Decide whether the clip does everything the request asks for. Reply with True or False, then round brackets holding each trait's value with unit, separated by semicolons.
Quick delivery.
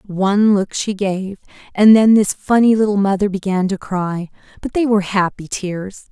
False (175 wpm)